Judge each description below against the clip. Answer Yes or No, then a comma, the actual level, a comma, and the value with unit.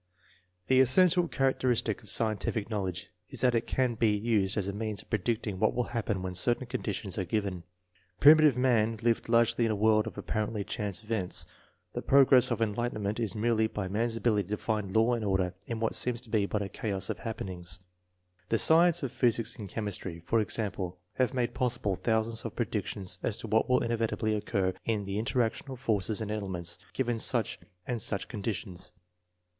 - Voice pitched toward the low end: Yes, low, 110 Hz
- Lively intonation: No, average, 2.8 semitones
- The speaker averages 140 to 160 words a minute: No, average, 190 wpm